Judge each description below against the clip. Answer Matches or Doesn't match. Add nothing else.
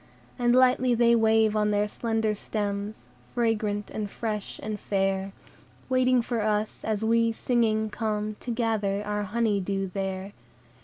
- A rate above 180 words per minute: Doesn't match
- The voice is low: Doesn't match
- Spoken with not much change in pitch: Matches